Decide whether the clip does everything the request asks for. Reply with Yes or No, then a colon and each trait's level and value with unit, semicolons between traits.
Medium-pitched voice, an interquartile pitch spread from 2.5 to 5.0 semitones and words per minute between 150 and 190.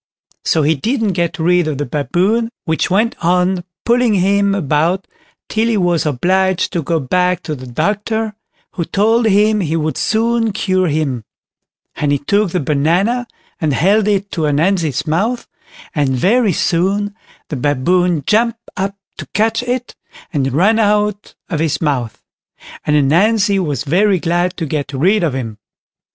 No: medium, 180 Hz; wide, 5.4 semitones; average, 160 wpm